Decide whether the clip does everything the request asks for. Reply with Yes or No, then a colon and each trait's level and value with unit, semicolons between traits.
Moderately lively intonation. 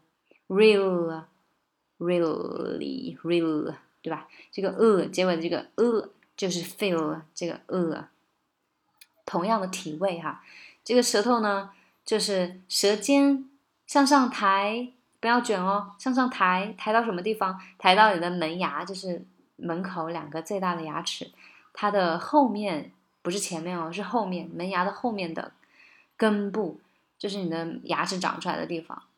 Yes: average, 4.1 semitones